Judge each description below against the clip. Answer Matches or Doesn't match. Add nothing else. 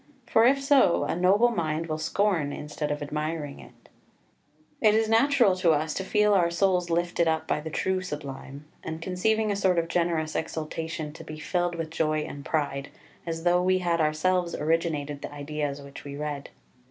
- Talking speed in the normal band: Matches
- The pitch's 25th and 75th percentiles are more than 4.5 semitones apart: Doesn't match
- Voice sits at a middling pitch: Matches